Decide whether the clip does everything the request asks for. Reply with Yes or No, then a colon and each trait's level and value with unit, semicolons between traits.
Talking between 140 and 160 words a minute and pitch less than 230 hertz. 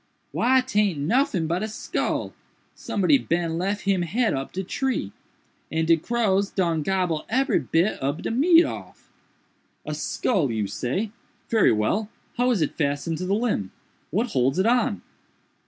Yes: average, 145 wpm; high, 190 Hz